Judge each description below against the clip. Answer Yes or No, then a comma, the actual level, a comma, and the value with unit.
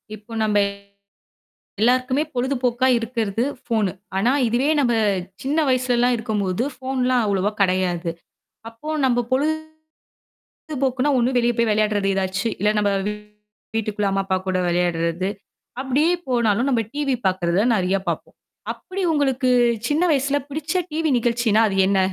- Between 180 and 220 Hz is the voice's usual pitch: No, high, 235 Hz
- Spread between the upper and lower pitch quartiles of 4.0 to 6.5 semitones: Yes, average, 4.5 semitones